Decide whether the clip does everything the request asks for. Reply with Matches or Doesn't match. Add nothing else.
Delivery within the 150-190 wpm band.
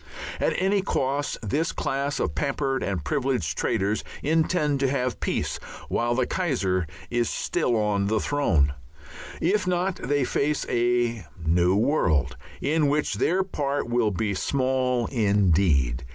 Doesn't match